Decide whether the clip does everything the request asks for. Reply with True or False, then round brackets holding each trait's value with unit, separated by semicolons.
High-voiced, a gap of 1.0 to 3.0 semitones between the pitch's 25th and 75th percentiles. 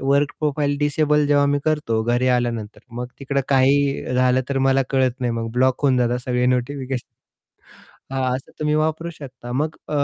False (135 Hz; 2.6 semitones)